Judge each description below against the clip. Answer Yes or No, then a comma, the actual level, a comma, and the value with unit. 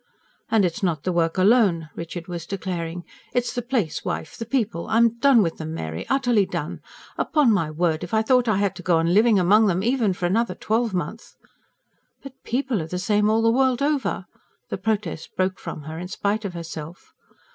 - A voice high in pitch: Yes, high, 200 Hz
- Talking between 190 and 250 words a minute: Yes, average, 200 wpm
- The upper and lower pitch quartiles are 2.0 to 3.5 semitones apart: No, average, 5.2 semitones